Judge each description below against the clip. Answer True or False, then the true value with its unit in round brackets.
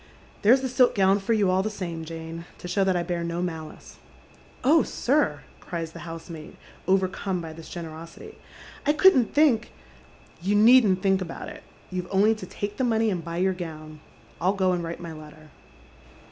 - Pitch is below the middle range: False (185 Hz)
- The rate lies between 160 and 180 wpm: False (190 wpm)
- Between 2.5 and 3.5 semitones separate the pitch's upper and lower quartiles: False (4.3 semitones)